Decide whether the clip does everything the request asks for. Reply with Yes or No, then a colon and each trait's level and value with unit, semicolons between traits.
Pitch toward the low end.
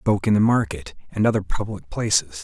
Yes: low, 100 Hz